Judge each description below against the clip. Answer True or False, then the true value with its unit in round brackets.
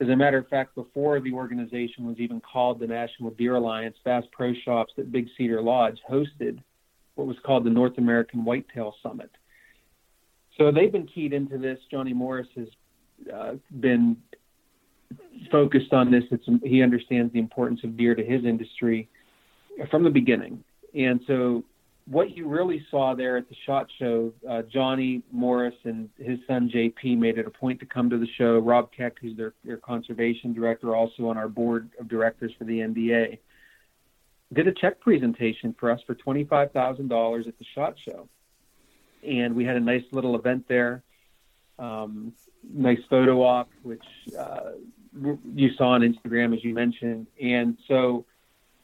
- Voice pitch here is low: True (120 Hz)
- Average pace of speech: True (165 wpm)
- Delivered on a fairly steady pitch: True (1.9 semitones)